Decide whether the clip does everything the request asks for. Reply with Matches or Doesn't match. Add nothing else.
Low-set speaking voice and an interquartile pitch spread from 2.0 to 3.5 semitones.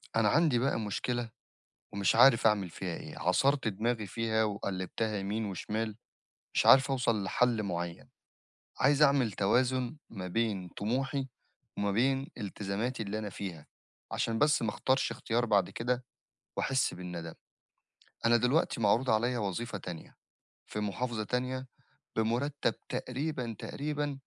Doesn't match